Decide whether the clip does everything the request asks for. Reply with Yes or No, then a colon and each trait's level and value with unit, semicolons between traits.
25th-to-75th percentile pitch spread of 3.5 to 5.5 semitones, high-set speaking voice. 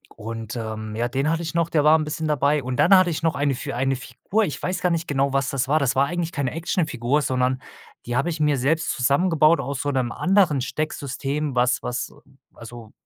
No: average, 4.0 semitones; medium, 140 Hz